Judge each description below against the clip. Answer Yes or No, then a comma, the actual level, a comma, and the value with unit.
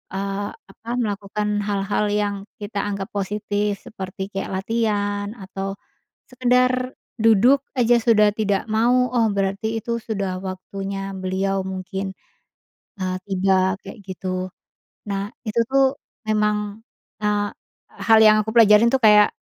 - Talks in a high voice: Yes, high, 205 Hz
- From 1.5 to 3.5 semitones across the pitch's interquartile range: Yes, narrow, 2.4 semitones